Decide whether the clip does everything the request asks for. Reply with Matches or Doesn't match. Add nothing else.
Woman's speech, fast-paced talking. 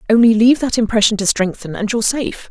Matches